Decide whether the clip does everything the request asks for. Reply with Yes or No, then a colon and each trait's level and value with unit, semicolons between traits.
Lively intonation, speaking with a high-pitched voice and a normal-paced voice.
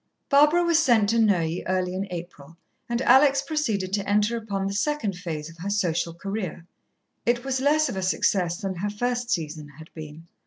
Yes: wide, 5.9 semitones; high, 200 Hz; average, 190 wpm